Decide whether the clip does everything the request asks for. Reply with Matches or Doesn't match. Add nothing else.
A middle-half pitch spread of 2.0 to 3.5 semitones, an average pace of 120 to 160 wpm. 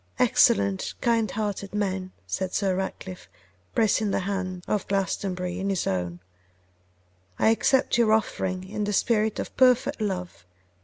Matches